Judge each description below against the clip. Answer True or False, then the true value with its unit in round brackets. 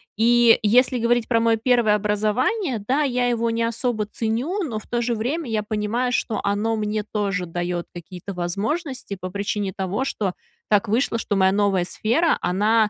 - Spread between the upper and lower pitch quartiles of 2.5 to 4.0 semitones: True (3.0 semitones)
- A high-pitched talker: True (220 Hz)